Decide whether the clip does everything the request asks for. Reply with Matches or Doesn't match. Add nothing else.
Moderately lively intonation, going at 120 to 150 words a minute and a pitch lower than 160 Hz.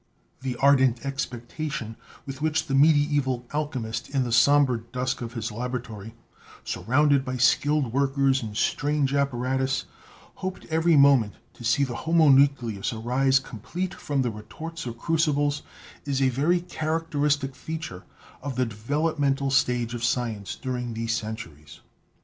Matches